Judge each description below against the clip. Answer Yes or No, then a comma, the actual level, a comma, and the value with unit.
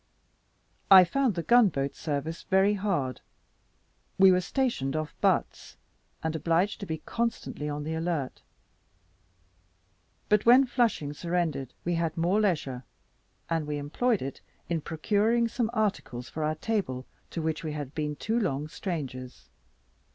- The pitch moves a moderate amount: No, wide, 5.8 semitones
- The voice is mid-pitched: Yes, medium, 165 Hz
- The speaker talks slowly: No, average, 145 wpm